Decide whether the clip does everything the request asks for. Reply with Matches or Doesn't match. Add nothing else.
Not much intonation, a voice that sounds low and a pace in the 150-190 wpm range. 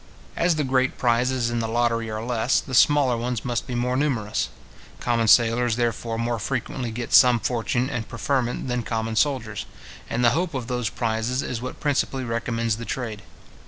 Matches